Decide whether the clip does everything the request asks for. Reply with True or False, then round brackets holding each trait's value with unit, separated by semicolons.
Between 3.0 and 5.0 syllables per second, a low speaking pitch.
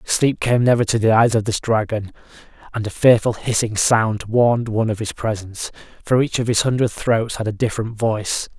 False (5.5 syllables/s; 110 Hz)